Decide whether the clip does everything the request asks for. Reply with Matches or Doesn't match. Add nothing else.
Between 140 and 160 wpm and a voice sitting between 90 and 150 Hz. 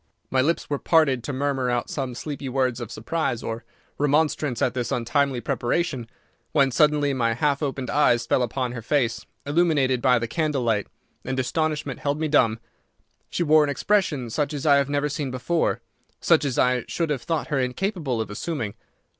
Doesn't match